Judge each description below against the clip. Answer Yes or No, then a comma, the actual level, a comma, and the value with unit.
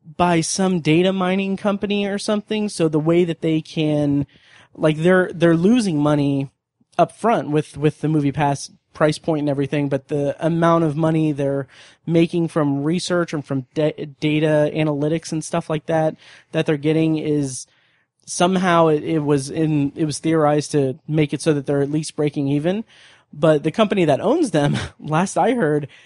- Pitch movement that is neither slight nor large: No, narrow, 2.2 semitones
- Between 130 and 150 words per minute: No, average, 180 wpm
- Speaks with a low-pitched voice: No, medium, 155 Hz